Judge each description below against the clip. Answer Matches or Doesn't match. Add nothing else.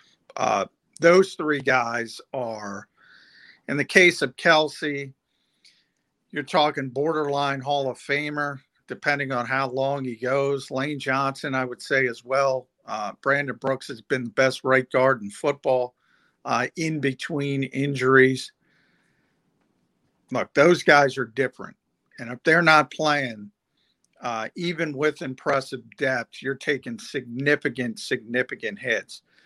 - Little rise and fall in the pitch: Matches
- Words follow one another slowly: Matches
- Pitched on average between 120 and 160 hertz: Matches